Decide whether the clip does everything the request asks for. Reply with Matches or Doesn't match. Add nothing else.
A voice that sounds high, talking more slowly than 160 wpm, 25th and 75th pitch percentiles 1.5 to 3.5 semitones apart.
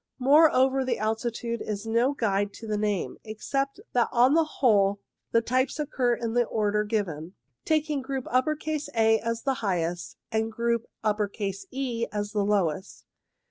Doesn't match